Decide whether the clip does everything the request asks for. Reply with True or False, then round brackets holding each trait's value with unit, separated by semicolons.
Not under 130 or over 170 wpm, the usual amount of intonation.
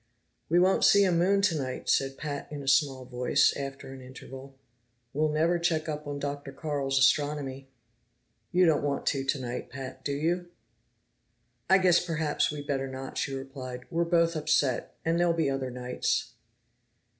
True (165 wpm; 3.6 semitones)